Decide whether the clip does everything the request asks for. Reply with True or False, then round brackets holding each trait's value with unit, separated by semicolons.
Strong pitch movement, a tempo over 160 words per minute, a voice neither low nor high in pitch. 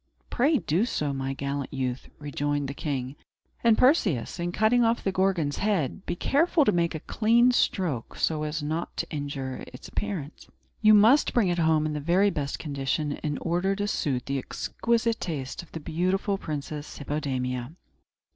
True (6.2 semitones; 175 wpm; 160 Hz)